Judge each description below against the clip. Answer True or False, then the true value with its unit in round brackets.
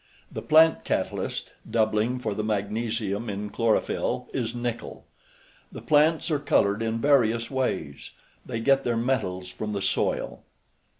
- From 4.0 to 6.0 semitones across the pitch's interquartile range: False (3.3 semitones)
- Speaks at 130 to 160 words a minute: True (135 wpm)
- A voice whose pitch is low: True (115 Hz)